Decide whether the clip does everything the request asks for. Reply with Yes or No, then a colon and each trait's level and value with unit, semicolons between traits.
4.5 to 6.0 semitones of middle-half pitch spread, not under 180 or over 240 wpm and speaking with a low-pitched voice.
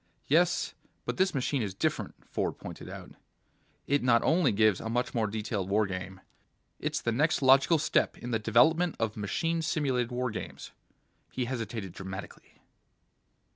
No: average, 5.0 semitones; average, 155 wpm; low, 120 Hz